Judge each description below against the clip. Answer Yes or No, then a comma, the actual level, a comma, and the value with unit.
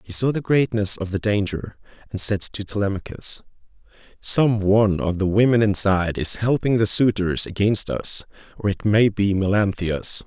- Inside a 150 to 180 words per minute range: Yes, average, 165 wpm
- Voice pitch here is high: No, low, 105 Hz